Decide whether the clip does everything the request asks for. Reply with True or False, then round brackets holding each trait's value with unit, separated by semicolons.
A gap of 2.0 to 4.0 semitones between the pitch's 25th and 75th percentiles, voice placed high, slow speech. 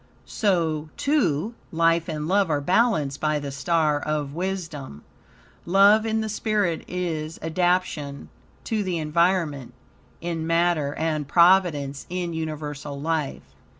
False (3.5 semitones; 165 Hz; 120 wpm)